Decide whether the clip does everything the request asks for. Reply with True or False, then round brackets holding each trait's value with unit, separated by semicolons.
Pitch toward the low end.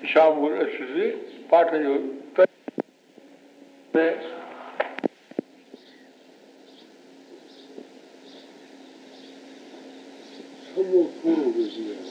False (185 Hz)